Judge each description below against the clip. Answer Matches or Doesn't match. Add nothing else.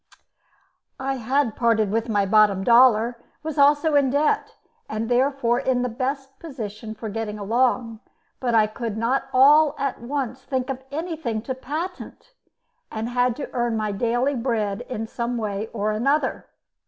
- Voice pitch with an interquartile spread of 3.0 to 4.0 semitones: Matches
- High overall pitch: Matches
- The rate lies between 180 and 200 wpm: Doesn't match